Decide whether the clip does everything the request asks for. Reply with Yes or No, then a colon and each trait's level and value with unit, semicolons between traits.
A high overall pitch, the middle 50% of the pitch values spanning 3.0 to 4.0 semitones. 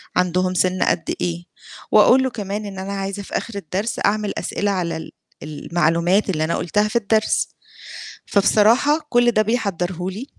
Yes: high, 195 Hz; average, 3.3 semitones